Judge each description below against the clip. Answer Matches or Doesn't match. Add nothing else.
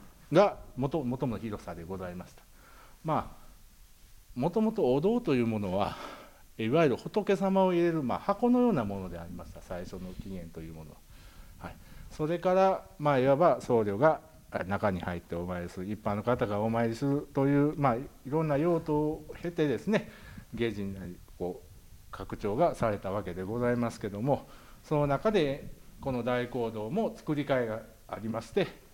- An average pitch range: Doesn't match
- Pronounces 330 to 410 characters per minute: Doesn't match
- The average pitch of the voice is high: Doesn't match